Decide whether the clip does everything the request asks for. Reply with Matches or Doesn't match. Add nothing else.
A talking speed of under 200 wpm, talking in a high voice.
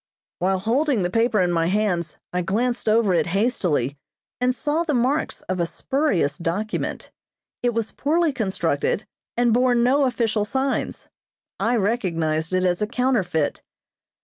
Matches